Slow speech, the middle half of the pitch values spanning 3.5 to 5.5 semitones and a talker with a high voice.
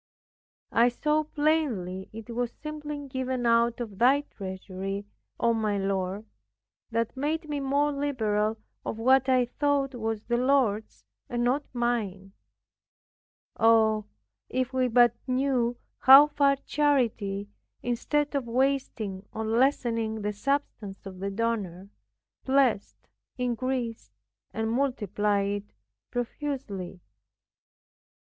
Yes: slow, 110 wpm; average, 4.5 semitones; high, 240 Hz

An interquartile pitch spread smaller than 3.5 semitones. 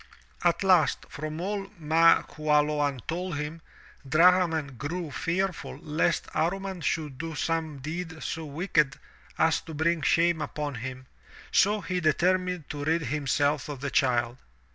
Yes: average, 2.9 semitones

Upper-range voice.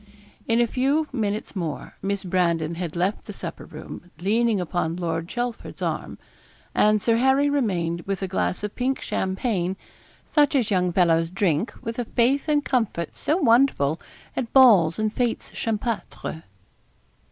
Yes: high, 210 Hz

